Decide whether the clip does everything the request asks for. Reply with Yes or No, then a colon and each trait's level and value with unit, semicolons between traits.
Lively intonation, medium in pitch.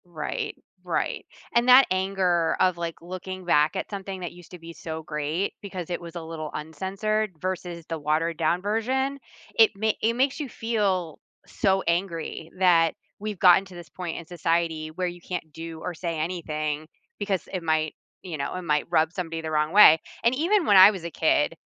No: average, 3.2 semitones; medium, 175 Hz